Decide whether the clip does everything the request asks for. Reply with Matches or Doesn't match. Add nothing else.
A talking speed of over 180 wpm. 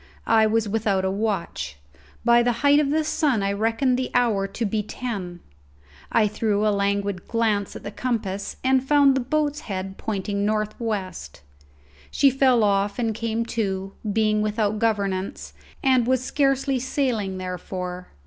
Doesn't match